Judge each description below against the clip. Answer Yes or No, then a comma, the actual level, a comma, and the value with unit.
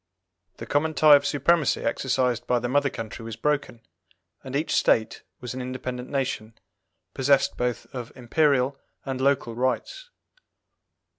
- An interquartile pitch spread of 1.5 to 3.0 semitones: Yes, narrow, 2.6 semitones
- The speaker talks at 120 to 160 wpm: Yes, average, 140 wpm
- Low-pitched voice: Yes, low, 130 Hz